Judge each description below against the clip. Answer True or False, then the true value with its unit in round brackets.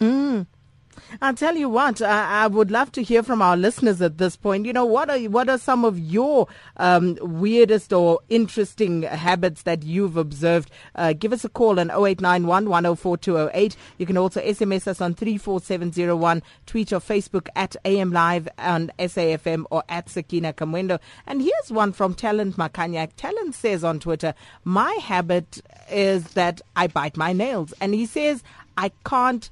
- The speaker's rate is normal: True (185 wpm)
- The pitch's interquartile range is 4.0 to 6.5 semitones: True (4.4 semitones)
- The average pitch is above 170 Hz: True (190 Hz)